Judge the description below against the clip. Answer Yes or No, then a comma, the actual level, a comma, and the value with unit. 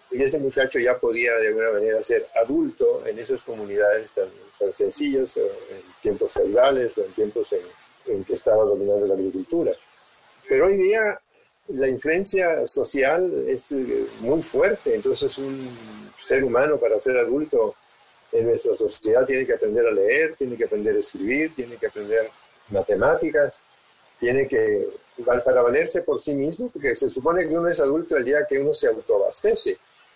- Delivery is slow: No, average, 170 wpm